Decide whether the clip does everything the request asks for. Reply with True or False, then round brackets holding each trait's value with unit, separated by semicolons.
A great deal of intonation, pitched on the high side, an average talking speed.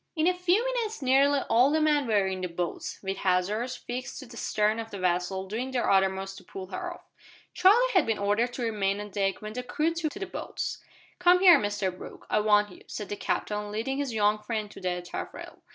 False (6.4 semitones; 215 Hz; 230 wpm)